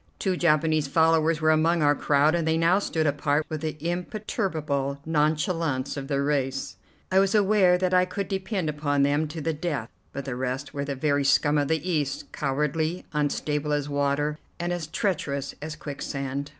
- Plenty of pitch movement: No, average, 2.7 semitones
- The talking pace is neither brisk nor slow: Yes, average, 180 wpm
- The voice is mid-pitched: Yes, medium, 150 Hz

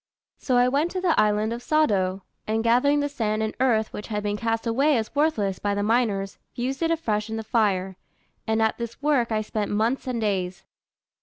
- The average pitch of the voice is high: Yes, high, 225 Hz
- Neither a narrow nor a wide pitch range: Yes, average, 3.5 semitones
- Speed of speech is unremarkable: No, fast, 210 wpm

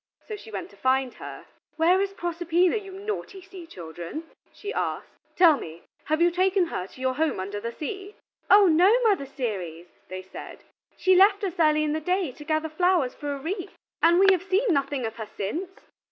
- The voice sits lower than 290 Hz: No, very high, 325 Hz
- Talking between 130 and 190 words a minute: No, average, 200 wpm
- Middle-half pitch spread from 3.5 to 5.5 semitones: No, wide, 6.6 semitones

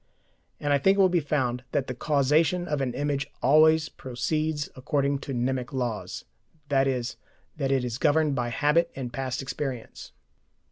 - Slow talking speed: No, average, 160 wpm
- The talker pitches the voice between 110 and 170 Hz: Yes, medium, 140 Hz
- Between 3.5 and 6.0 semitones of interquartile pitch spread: No, average, 2.9 semitones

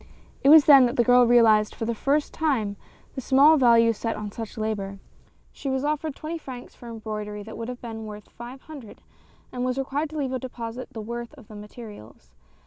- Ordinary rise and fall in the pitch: Yes, average, 3.7 semitones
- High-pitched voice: Yes, high, 240 Hz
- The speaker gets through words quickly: Yes, fast, 215 wpm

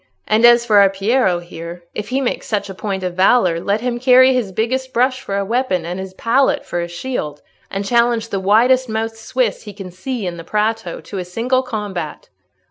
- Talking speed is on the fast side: Yes, fast, 210 wpm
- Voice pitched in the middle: No, high, 215 Hz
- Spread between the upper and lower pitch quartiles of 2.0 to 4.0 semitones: No, average, 4.7 semitones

